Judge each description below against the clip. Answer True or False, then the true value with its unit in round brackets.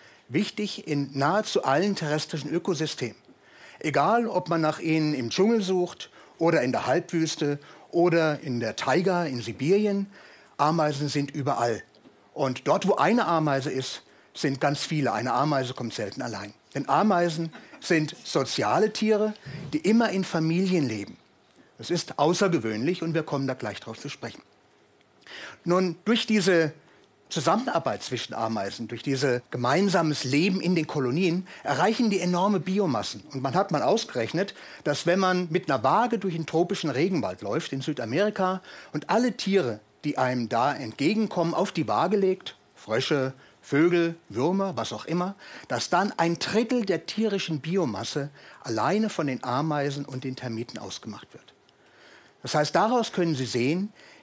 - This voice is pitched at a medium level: True (165 Hz)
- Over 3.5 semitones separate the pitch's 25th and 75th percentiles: True (5.2 semitones)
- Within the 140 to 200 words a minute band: True (150 wpm)